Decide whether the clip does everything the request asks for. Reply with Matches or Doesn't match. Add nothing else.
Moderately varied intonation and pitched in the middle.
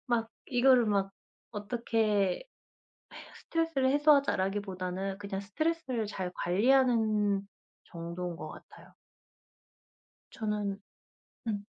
Doesn't match